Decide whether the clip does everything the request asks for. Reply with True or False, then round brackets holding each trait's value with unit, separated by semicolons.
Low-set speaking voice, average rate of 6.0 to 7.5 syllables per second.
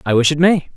False (155 Hz; 6.5 syllables/s)